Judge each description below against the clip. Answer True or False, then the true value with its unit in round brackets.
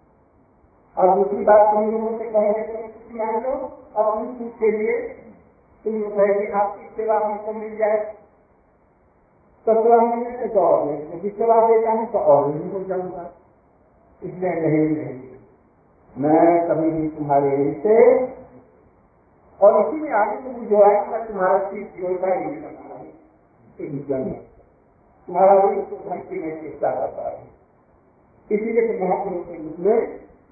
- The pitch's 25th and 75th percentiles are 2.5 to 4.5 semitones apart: True (3.4 semitones)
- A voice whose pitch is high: True (210 Hz)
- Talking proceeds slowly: True (90 wpm)